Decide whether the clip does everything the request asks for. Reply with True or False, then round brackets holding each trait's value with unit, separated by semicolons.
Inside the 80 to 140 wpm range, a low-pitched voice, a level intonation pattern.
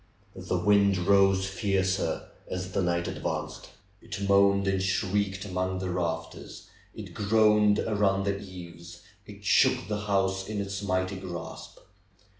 True (135 wpm; 95 Hz; 1.4 semitones)